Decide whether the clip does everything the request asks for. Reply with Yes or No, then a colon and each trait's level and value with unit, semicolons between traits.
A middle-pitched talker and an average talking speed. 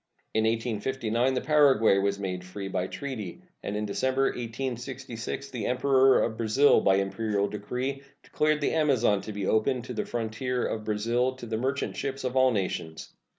No: low, 120 Hz; average, 170 wpm